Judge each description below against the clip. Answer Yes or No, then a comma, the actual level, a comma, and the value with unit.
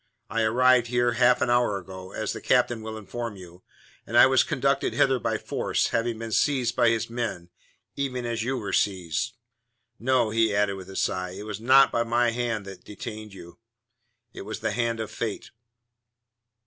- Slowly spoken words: No, average, 185 wpm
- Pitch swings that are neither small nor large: Yes, average, 3.0 semitones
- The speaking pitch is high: No, low, 115 Hz